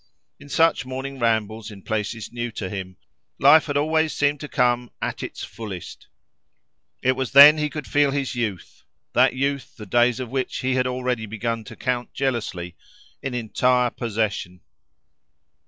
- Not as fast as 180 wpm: Yes, average, 160 wpm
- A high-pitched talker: No, low, 125 Hz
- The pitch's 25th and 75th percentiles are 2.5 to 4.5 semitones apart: Yes, average, 3.7 semitones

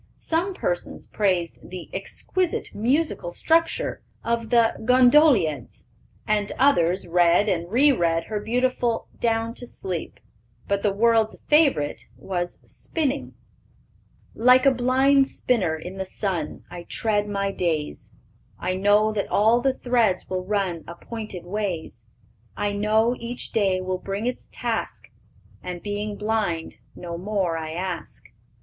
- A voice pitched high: Yes, high, 205 Hz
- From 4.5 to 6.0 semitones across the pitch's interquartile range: Yes, average, 5.1 semitones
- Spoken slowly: Yes, slow, 130 wpm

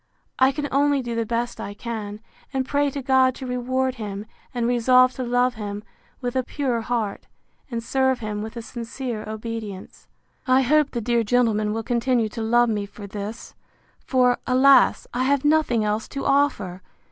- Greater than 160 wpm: Yes, average, 180 wpm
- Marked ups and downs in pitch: No, average, 3.0 semitones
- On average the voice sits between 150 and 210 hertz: No, high, 240 Hz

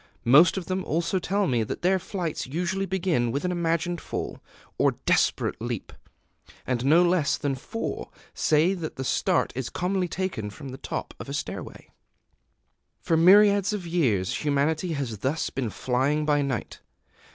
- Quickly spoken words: No, average, 165 wpm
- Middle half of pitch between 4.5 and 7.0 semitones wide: Yes, average, 5.3 semitones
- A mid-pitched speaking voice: Yes, medium, 160 Hz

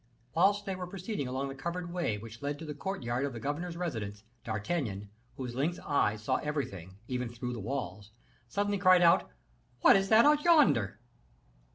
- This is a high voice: No, medium, 140 Hz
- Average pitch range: No, wide, 7.9 semitones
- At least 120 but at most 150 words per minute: No, average, 180 wpm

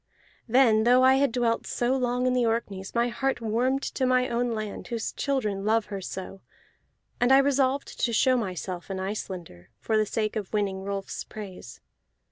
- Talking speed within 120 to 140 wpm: No, average, 180 wpm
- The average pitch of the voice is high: Yes, high, 230 Hz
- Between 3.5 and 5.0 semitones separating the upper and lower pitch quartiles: Yes, average, 4.2 semitones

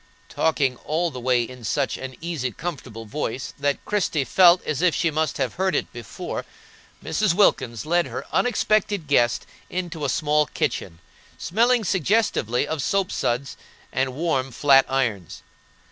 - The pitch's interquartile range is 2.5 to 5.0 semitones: No, wide, 5.4 semitones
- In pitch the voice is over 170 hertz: No, medium, 150 Hz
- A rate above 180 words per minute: No, average, 150 wpm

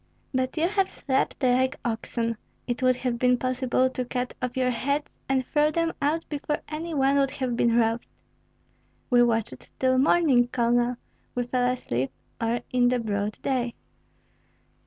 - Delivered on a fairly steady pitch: Yes, narrow, 2.2 semitones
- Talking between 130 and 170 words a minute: Yes, average, 160 wpm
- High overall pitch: Yes, very high, 250 Hz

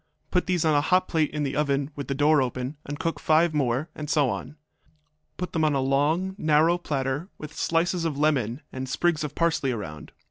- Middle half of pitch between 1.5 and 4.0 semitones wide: Yes, average, 3.2 semitones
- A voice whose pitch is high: No, medium, 150 Hz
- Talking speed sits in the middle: No, fast, 210 wpm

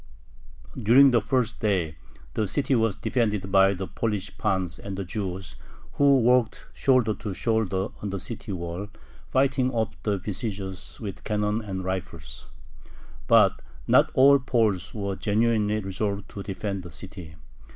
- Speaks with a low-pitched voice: Yes, low, 105 Hz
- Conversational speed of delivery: Yes, average, 145 wpm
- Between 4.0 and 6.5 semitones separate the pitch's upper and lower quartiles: No, average, 3.2 semitones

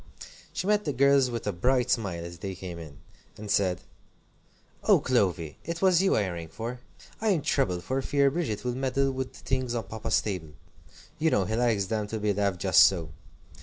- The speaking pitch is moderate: No, low, 110 Hz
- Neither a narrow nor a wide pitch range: No, wide, 6.2 semitones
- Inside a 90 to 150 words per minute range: No, fast, 205 wpm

